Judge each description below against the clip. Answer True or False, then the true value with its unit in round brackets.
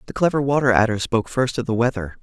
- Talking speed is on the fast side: True (245 wpm)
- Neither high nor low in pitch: False (120 Hz)